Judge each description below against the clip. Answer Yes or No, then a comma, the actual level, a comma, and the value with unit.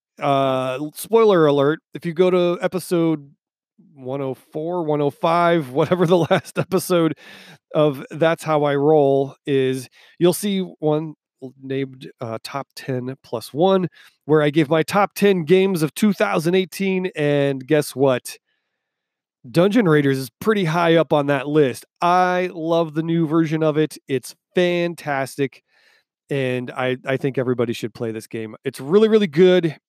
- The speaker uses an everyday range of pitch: Yes, average, 4.5 semitones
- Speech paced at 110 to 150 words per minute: Yes, average, 145 wpm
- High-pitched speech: No, medium, 155 Hz